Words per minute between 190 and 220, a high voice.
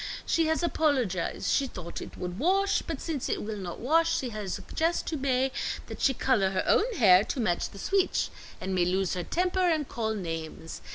Yes: fast, 205 wpm; high, 245 Hz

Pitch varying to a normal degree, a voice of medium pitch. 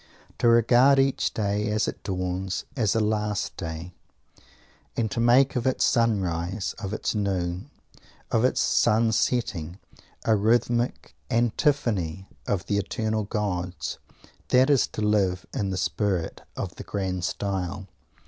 No: average, 4.0 semitones; low, 105 Hz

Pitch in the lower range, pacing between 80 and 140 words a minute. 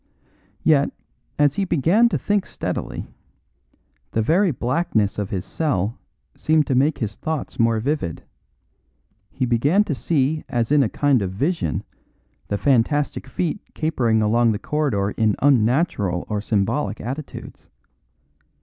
Yes: low, 130 Hz; slow, 135 wpm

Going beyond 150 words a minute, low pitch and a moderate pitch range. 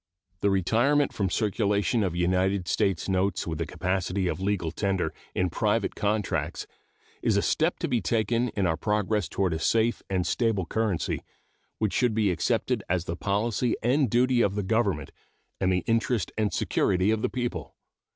Yes: average, 170 wpm; low, 100 Hz; average, 3.5 semitones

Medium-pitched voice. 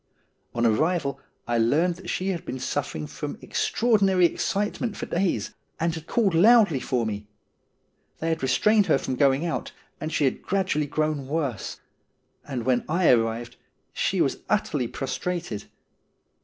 Yes: medium, 155 Hz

